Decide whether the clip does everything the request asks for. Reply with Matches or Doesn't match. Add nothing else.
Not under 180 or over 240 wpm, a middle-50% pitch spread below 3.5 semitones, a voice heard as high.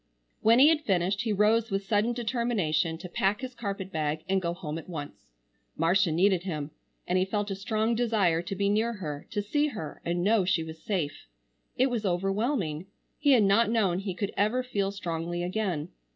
Doesn't match